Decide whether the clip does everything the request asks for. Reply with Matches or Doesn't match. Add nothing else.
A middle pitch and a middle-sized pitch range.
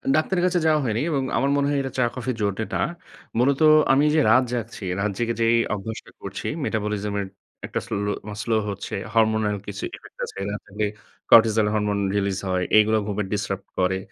Doesn't match